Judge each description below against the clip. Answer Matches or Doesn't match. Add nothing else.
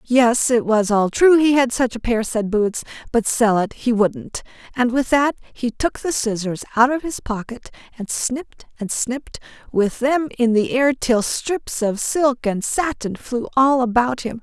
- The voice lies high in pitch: Matches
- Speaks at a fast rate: Doesn't match